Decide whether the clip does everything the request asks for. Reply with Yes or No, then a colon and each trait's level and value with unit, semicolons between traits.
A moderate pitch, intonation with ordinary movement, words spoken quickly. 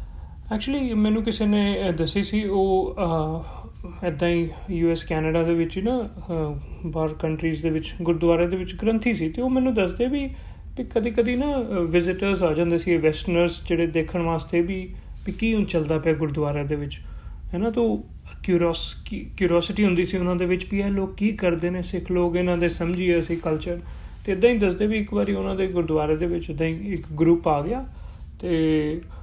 Yes: medium, 175 Hz; average, 3.5 semitones; fast, 185 wpm